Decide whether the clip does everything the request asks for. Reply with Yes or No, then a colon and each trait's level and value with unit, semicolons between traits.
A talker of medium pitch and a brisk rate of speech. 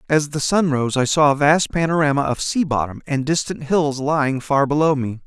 Yes: medium, 145 Hz; fast, 215 wpm